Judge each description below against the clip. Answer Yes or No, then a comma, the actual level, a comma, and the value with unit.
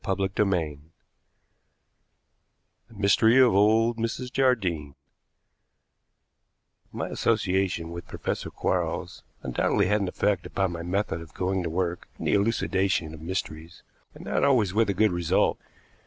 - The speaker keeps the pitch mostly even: No, average, 3.9 semitones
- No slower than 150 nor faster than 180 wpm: No, slow, 135 wpm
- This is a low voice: Yes, very low, 95 Hz